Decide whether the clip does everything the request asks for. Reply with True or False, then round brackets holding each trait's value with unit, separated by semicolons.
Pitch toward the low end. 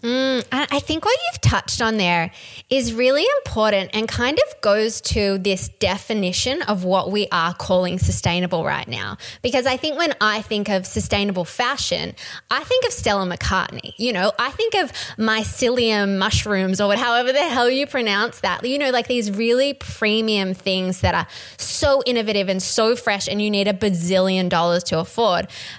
False (215 Hz)